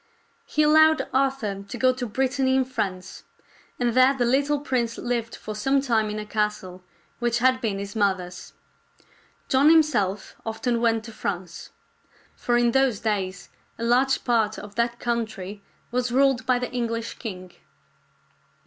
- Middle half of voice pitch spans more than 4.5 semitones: No, average, 3.6 semitones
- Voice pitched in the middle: No, high, 235 Hz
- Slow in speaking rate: No, average, 155 wpm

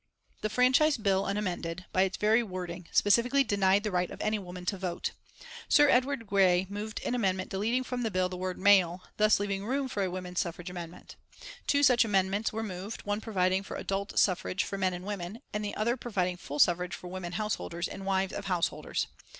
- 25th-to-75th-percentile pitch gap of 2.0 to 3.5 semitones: Yes, average, 2.9 semitones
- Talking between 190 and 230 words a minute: Yes, average, 200 wpm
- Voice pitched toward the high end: Yes, high, 195 Hz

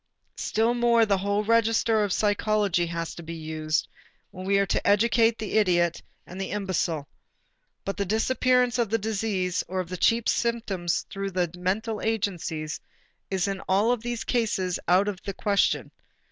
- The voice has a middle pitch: No, high, 200 Hz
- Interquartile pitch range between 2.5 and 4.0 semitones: Yes, average, 3.6 semitones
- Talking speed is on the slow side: No, average, 165 wpm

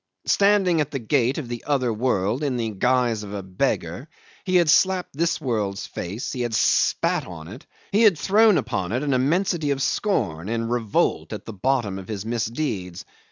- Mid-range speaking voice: No, low, 125 Hz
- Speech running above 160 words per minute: Yes, average, 190 wpm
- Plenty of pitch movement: Yes, wide, 6.4 semitones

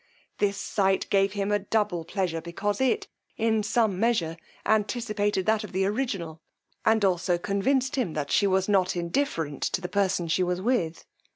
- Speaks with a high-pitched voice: Yes, high, 200 Hz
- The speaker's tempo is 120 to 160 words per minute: No, average, 170 wpm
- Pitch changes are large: No, average, 3.4 semitones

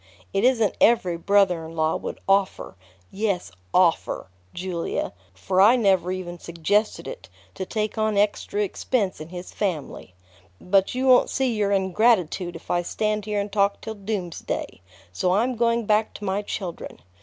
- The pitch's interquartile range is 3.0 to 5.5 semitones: Yes, average, 3.4 semitones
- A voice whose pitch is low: No, high, 200 Hz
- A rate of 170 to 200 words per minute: No, average, 160 wpm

